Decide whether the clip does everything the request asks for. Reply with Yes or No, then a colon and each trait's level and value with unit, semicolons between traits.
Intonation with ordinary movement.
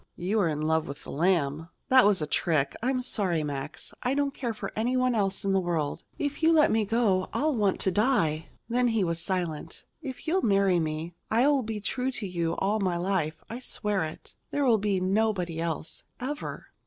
No: wide, 6.4 semitones